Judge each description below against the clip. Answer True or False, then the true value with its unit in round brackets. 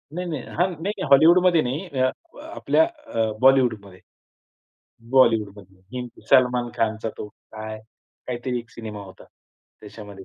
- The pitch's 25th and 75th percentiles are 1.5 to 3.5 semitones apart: False (4.3 semitones)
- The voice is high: False (120 Hz)